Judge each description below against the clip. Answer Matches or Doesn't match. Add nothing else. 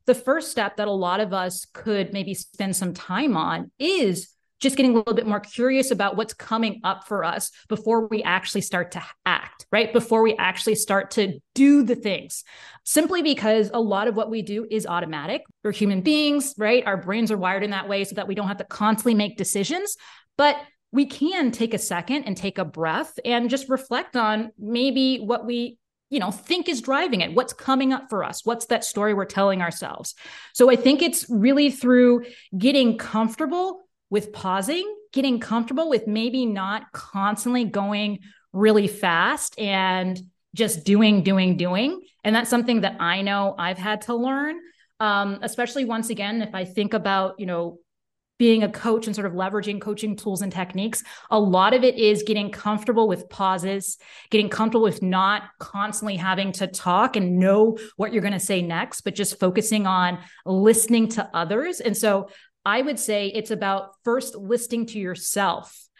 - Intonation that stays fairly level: Doesn't match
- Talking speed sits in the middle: Matches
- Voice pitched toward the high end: Matches